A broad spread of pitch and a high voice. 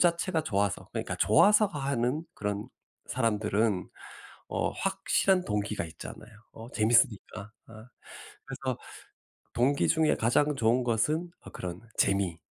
No: wide, 6.4 semitones; low, 115 Hz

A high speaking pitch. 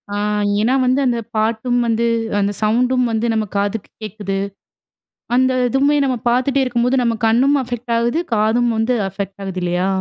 Yes: high, 235 Hz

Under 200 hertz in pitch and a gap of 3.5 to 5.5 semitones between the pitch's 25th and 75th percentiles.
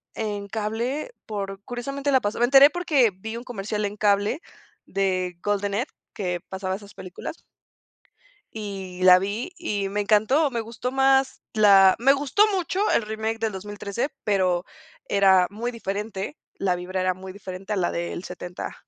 No: high, 205 Hz; average, 3.8 semitones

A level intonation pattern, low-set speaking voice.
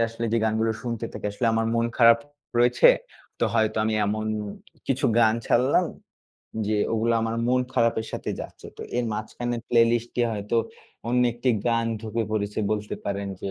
Yes: narrow, 1.5 semitones; low, 115 Hz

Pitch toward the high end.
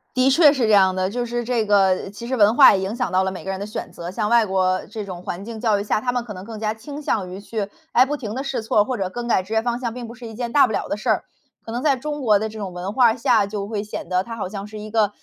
Yes: high, 220 Hz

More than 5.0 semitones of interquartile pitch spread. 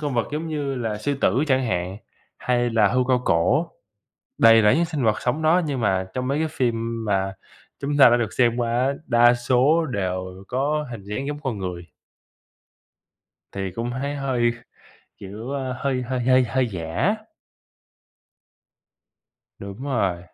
No: average, 4.7 semitones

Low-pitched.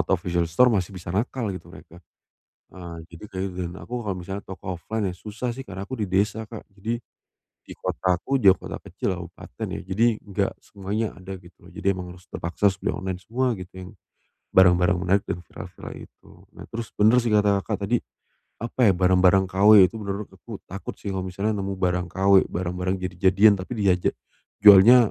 Yes: very low, 95 Hz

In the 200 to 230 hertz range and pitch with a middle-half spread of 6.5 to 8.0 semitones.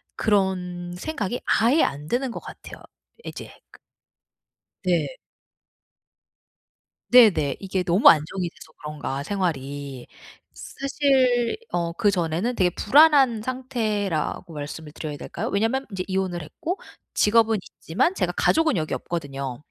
No: high, 190 Hz; wide, 7.1 semitones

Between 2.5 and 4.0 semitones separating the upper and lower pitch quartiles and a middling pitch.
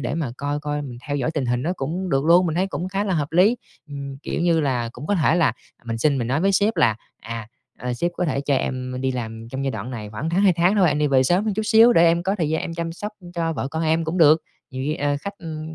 No: average, 4.7 semitones; medium, 155 Hz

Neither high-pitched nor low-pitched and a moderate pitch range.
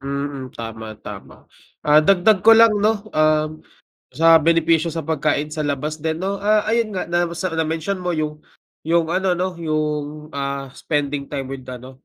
Yes: medium, 155 Hz; average, 3.4 semitones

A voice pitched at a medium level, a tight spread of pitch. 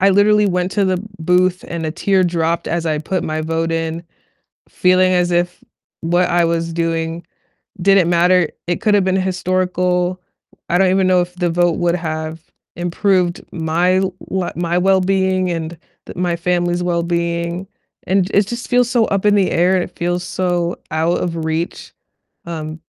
Yes: medium, 175 Hz; narrow, 1.7 semitones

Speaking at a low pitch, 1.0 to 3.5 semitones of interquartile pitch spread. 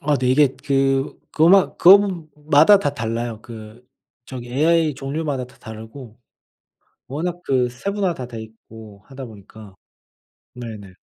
No: low, 130 Hz; average, 5.2 semitones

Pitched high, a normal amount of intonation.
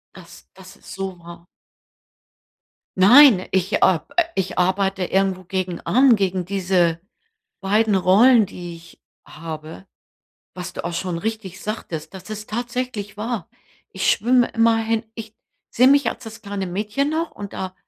Yes: high, 195 Hz; average, 3.6 semitones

